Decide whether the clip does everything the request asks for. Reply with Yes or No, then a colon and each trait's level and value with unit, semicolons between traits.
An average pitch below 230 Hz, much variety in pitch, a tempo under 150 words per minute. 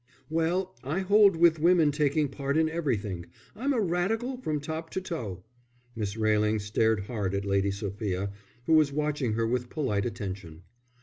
No: medium, 140 Hz; wide, 8.1 semitones; average, 165 wpm